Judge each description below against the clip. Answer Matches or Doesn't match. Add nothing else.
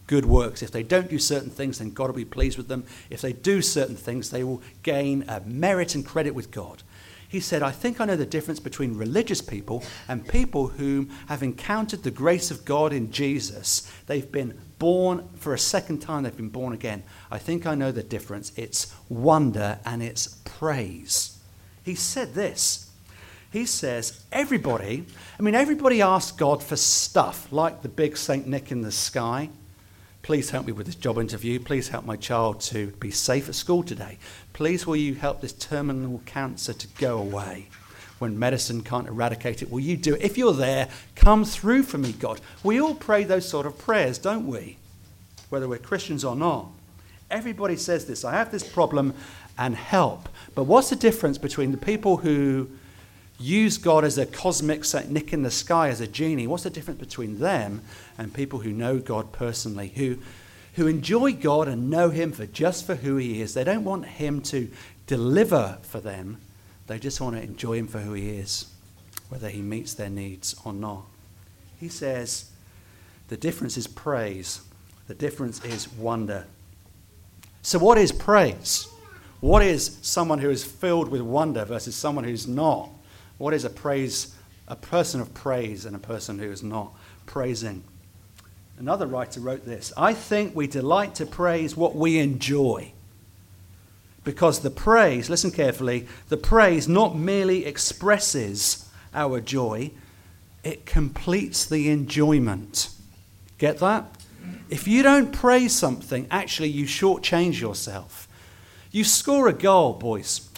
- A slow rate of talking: Doesn't match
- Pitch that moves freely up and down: Matches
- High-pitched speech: Doesn't match